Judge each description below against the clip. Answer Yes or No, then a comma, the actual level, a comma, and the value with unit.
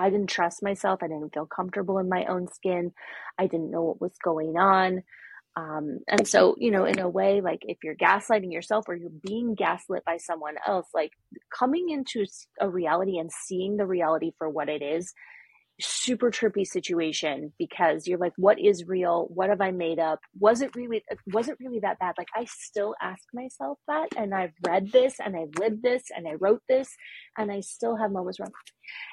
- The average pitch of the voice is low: No, high, 190 Hz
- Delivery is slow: No, average, 200 wpm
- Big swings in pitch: No, average, 4.1 semitones